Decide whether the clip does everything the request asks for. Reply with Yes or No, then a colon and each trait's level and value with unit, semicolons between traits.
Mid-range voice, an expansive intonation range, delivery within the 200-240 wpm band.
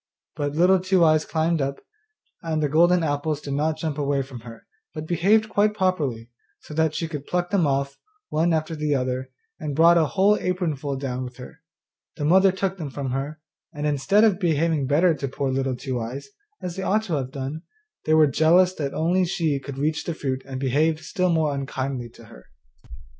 No: medium, 155 Hz; average, 3.9 semitones; fast, 205 wpm